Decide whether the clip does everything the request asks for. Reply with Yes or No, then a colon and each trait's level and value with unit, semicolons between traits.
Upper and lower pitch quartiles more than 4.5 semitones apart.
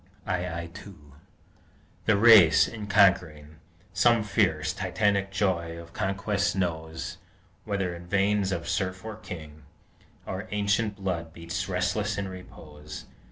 No: average, 3.3 semitones